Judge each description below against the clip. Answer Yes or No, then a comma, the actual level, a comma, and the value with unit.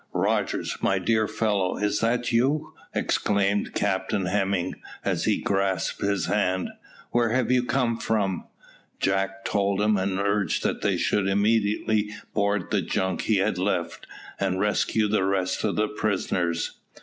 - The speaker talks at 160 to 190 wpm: No, average, 150 wpm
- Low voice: Yes, low, 100 Hz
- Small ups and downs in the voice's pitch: Yes, narrow, 2.1 semitones